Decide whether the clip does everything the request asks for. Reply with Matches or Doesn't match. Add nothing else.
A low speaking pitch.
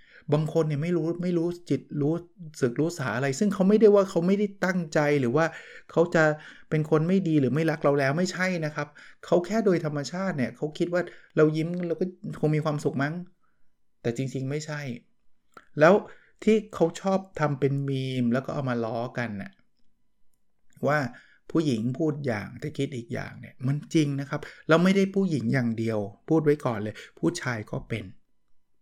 Doesn't match